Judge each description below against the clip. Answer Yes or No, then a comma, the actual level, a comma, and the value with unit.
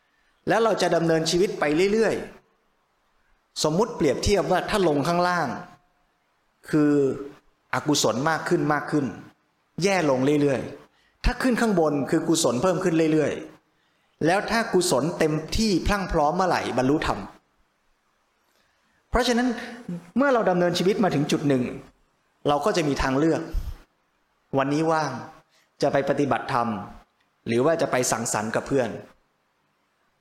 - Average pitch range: Yes, average, 4.2 semitones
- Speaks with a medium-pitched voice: Yes, medium, 160 Hz